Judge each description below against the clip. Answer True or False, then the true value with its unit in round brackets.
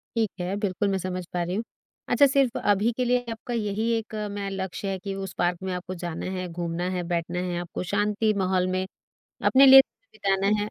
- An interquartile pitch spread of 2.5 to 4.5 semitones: True (3.1 semitones)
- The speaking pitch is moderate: False (195 Hz)